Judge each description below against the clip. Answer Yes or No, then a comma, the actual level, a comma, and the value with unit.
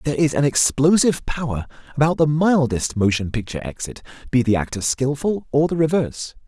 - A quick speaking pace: No, average, 165 wpm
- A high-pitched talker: No, medium, 140 Hz